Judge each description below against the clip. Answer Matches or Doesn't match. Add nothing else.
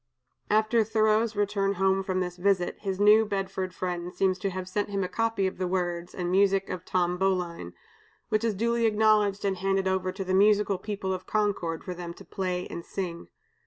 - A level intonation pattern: Matches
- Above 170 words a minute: Matches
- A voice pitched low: Doesn't match